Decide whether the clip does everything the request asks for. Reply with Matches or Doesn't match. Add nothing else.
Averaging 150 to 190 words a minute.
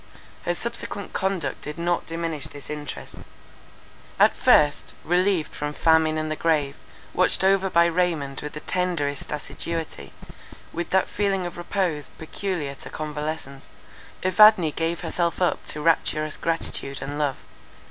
Doesn't match